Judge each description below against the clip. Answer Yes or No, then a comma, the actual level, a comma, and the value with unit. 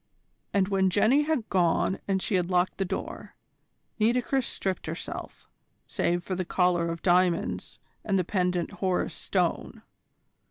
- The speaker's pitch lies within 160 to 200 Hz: Yes, medium, 185 Hz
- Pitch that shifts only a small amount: Yes, narrow, 2.2 semitones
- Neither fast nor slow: Yes, average, 145 wpm